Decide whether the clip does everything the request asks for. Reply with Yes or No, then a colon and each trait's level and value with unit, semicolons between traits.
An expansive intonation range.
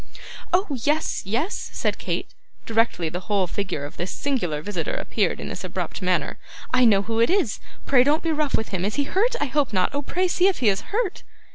Yes: wide, 7.9 semitones